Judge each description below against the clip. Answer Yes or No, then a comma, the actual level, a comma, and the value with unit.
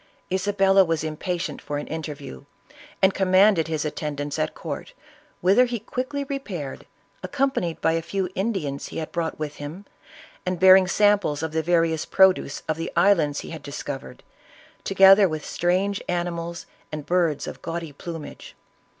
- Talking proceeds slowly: No, average, 155 wpm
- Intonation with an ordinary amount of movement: Yes, average, 3.7 semitones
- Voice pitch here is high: No, medium, 170 Hz